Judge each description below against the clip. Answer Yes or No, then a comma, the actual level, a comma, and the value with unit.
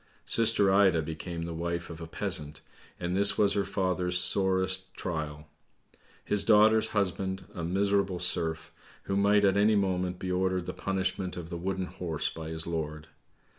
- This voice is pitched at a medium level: No, very low, 95 Hz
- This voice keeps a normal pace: Yes, average, 165 wpm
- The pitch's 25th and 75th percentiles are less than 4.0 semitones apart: Yes, average, 2.8 semitones